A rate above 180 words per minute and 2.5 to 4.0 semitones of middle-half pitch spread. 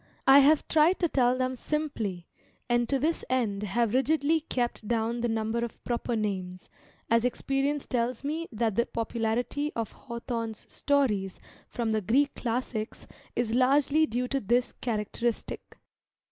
No: average, 145 wpm; average, 3.6 semitones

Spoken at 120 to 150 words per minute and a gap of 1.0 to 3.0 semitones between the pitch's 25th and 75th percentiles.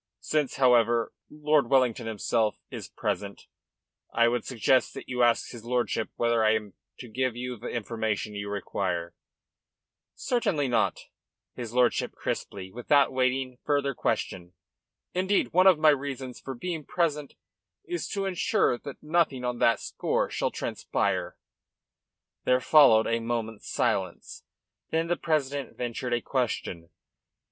No: average, 140 wpm; average, 3.9 semitones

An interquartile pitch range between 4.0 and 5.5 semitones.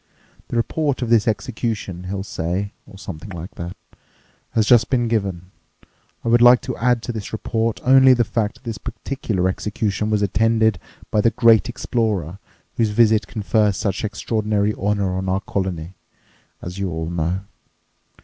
No: average, 3.4 semitones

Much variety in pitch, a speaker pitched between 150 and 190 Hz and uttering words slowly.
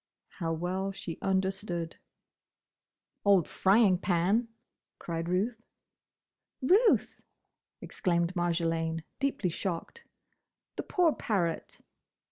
No: average, 3.4 semitones; medium, 185 Hz; slow, 85 wpm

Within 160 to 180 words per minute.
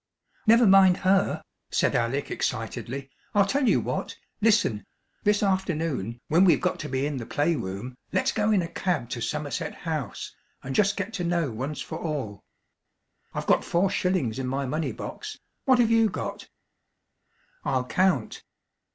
Yes: average, 165 wpm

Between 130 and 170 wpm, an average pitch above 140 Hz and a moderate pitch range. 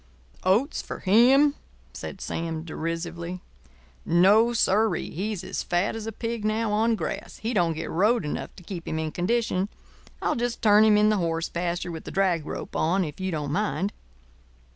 No: average, 185 wpm; high, 190 Hz; average, 4.4 semitones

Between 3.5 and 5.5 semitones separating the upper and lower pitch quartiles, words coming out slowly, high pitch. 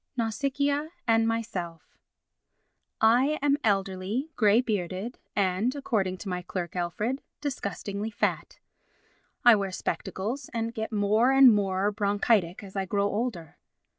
Yes: average, 3.8 semitones; slow, 125 wpm; high, 210 Hz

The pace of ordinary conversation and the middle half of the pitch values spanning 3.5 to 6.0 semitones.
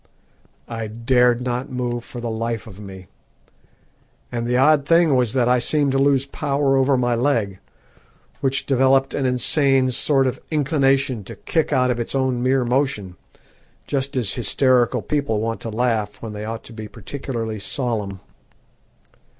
No: average, 160 wpm; average, 3.0 semitones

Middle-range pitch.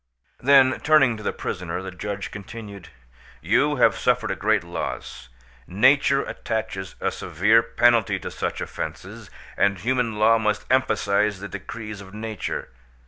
No: low, 105 Hz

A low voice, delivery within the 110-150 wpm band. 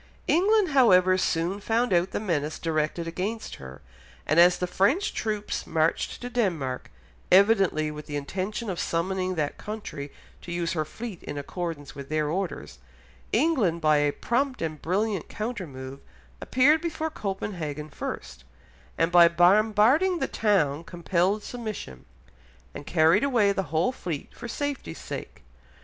No: medium, 185 Hz; average, 145 wpm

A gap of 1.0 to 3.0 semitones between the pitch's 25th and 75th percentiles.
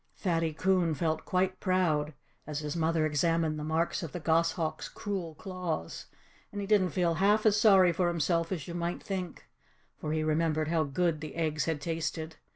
Yes: narrow, 2.6 semitones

